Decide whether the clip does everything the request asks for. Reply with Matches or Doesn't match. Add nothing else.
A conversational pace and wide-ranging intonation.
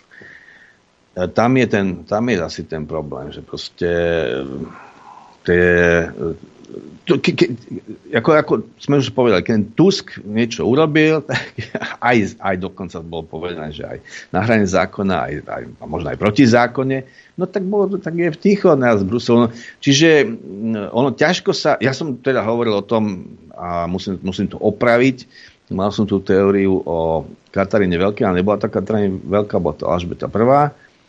Matches